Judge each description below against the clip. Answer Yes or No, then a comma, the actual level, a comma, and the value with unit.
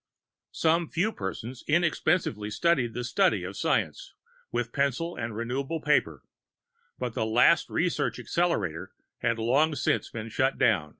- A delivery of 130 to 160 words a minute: Yes, slow, 135 wpm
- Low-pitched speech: Yes, low, 125 Hz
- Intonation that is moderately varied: No, wide, 6.3 semitones